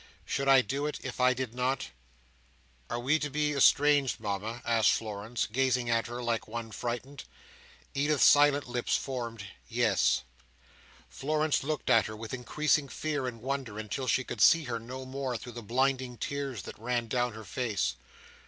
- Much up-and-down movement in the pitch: No, average, 3.1 semitones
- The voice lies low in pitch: Yes, low, 125 Hz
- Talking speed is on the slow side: No, average, 170 wpm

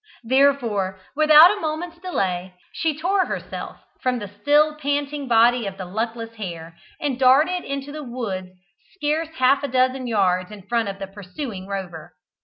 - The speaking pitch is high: Yes, very high, 250 Hz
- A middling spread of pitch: No, wide, 7.0 semitones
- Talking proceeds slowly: No, average, 160 wpm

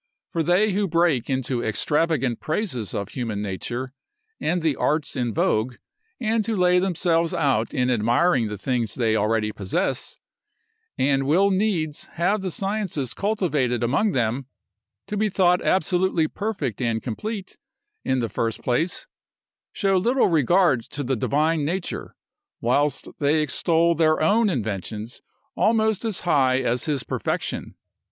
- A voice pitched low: No, medium, 150 Hz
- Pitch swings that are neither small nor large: No, wide, 7.0 semitones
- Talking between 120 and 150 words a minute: Yes, average, 140 wpm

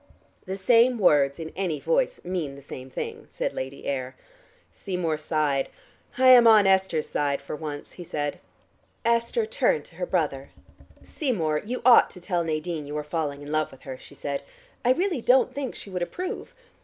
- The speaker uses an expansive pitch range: Yes, wide, 8.2 semitones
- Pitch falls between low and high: Yes, medium, 170 Hz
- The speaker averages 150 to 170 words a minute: No, average, 180 wpm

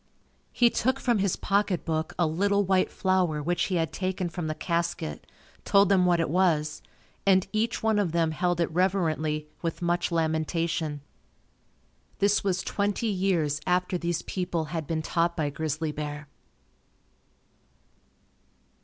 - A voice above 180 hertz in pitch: No, medium, 175 Hz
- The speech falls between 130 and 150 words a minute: Yes, average, 145 wpm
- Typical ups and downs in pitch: Yes, average, 3.2 semitones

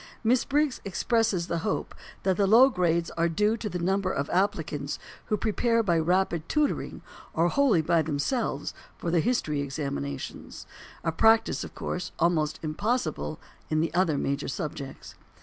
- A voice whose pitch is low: No, medium, 175 Hz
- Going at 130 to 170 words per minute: Yes, average, 155 wpm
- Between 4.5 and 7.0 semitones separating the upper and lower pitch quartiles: Yes, wide, 5.5 semitones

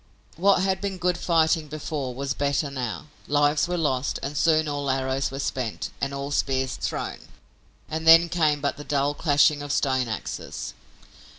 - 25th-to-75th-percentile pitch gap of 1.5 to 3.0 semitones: Yes, average, 2.7 semitones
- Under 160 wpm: No, average, 170 wpm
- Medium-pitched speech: Yes, medium, 145 Hz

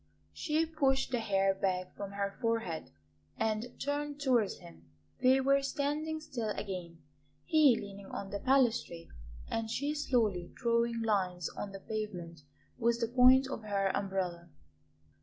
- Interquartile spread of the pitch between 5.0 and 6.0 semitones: Yes, wide, 5.5 semitones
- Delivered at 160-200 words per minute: No, average, 140 wpm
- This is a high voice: Yes, high, 225 Hz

